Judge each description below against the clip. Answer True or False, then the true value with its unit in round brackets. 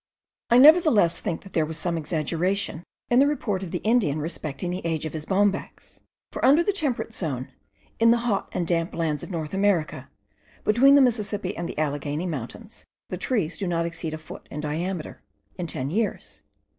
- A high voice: False (180 Hz)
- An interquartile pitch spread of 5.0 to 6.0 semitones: True (5.3 semitones)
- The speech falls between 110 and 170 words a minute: False (190 wpm)